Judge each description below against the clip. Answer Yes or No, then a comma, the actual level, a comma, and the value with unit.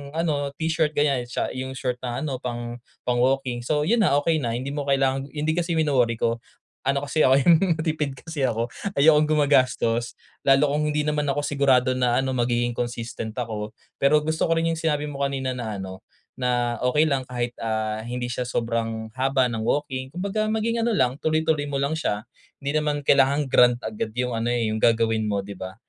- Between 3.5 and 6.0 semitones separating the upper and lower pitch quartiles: Yes, average, 3.8 semitones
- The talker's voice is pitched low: Yes, low, 130 Hz